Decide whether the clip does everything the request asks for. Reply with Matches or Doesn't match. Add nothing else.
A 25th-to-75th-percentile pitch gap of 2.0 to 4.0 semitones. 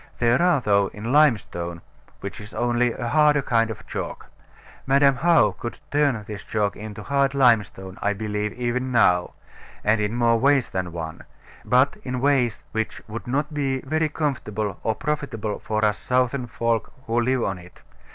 Doesn't match